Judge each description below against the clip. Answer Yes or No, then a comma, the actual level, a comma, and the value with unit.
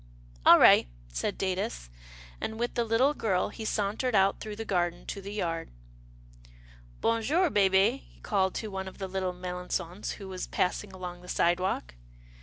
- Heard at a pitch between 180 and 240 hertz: Yes, high, 190 Hz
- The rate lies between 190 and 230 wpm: No, average, 170 wpm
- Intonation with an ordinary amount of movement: Yes, average, 3.3 semitones